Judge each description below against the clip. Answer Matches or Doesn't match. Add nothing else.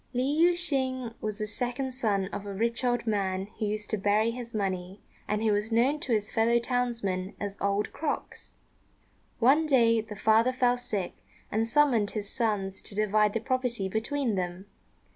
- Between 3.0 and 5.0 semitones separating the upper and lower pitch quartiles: Matches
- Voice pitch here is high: Matches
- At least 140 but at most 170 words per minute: Doesn't match